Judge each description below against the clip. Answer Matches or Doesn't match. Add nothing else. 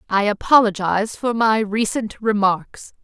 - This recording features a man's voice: Doesn't match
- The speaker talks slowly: Matches